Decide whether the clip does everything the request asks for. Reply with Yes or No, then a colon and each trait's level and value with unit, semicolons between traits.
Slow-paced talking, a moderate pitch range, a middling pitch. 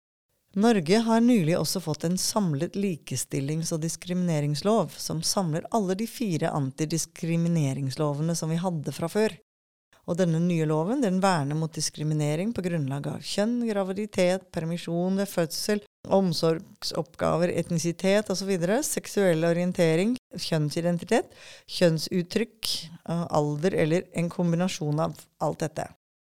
Yes: slow, 115 wpm; average, 3.4 semitones; medium, 170 Hz